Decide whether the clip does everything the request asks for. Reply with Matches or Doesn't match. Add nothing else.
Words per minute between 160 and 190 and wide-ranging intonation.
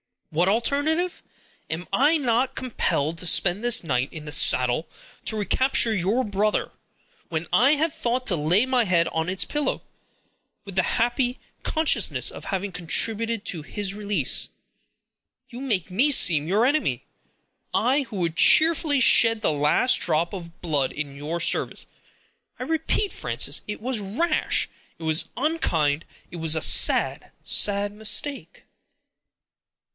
Doesn't match